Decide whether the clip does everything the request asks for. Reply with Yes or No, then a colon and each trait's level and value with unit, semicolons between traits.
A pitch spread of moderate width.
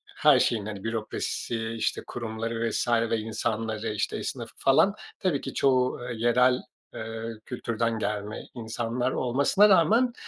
No: narrow, 2.3 semitones